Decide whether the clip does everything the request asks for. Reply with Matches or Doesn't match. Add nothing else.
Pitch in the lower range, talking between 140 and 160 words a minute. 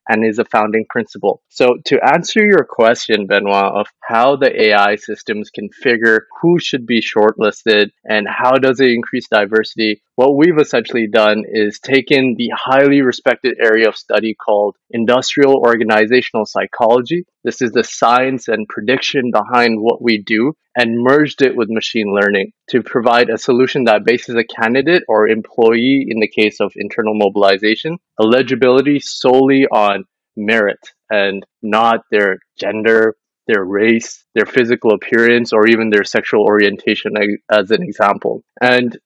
Matches